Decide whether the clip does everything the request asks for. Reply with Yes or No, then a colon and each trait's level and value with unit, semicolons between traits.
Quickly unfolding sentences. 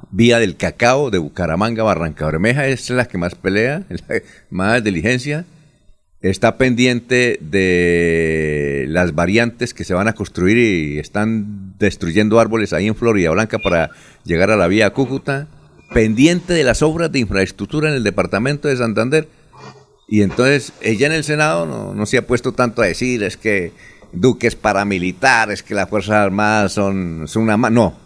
No: average, 170 wpm